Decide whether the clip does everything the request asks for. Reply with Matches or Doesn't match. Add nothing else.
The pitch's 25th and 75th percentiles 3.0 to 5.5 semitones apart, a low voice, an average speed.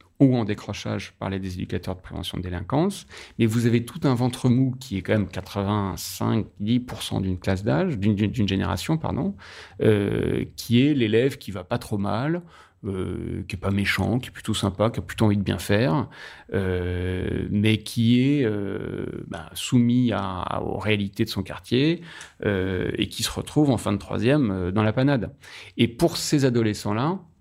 Matches